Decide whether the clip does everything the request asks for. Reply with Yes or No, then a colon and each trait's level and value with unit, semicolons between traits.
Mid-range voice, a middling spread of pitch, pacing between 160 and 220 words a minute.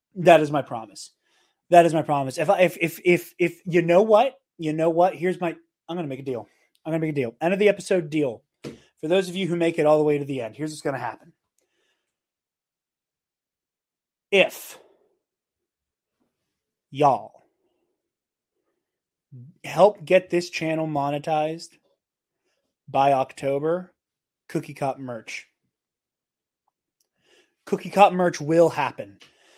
No: medium, 165 Hz; average, 3.3 semitones; average, 145 wpm